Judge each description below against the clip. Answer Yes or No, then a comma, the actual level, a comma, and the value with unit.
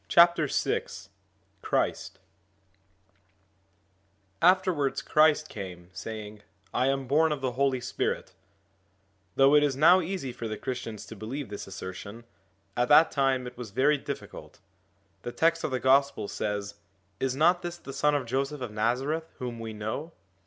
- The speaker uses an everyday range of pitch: Yes, average, 5.0 semitones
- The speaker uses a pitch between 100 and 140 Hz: Yes, low, 135 Hz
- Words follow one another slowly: No, average, 145 wpm